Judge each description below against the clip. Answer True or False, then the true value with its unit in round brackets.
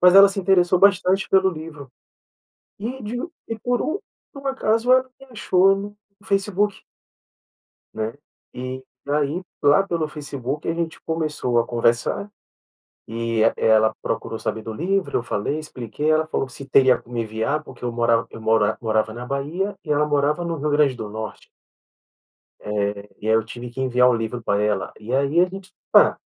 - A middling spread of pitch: False (7.9 semitones)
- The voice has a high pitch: False (145 Hz)